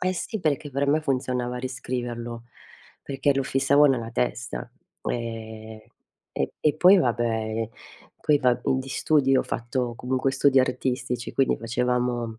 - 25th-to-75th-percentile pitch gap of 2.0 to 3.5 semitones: Yes, narrow, 2.4 semitones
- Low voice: Yes, low, 125 Hz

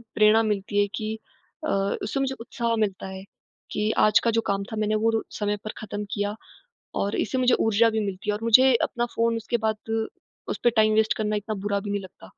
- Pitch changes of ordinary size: No, narrow, 2.0 semitones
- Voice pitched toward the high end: Yes, high, 215 Hz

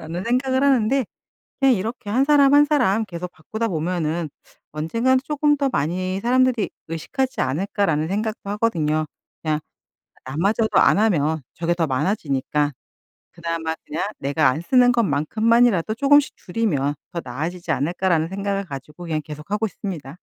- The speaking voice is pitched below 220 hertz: Yes, high, 190 Hz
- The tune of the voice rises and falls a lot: Yes, wide, 6.8 semitones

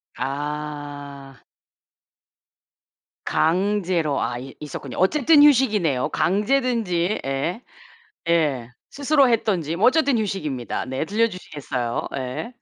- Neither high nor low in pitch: Yes, medium, 170 Hz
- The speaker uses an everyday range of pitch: No, wide, 8.1 semitones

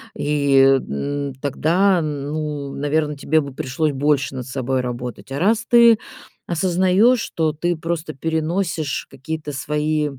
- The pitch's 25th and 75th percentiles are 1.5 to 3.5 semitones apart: Yes, average, 3.2 semitones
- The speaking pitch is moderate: Yes, medium, 150 Hz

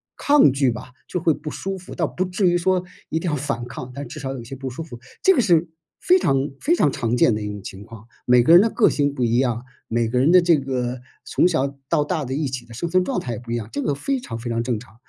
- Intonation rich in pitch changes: Yes, wide, 6.3 semitones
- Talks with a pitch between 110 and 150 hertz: Yes, low, 135 Hz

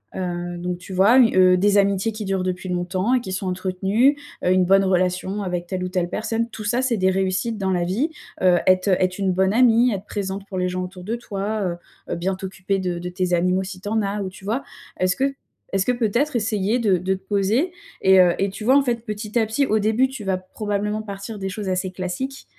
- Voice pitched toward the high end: Yes, high, 195 Hz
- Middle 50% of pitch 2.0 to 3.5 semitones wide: Yes, average, 2.9 semitones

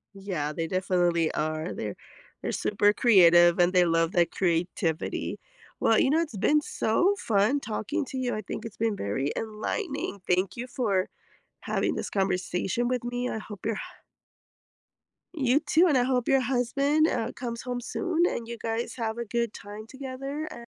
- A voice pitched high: Yes, high, 225 Hz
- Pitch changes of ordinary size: No, wide, 5.7 semitones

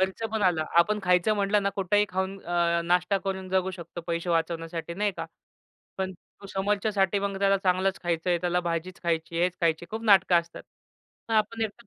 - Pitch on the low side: No, medium, 185 Hz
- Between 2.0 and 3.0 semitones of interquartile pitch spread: Yes, narrow, 2.6 semitones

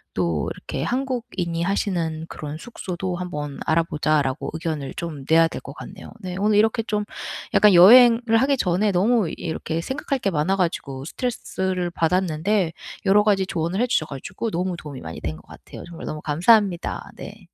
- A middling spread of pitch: Yes, average, 4.7 semitones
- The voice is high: No, medium, 180 Hz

